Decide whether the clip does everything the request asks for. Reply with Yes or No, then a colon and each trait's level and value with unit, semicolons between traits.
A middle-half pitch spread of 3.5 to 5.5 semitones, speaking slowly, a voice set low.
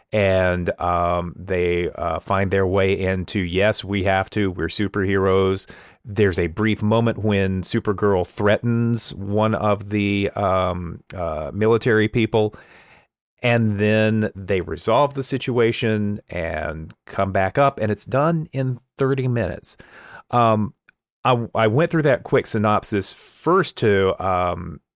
No: average, 3.1 semitones; slow, 130 wpm; low, 105 Hz